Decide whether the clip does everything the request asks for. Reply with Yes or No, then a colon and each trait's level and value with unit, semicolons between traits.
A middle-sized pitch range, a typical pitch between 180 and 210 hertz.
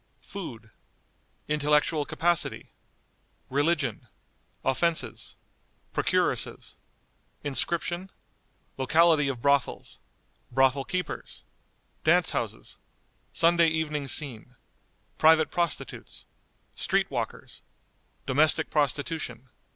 No: average, 3.7 semitones; medium, 150 Hz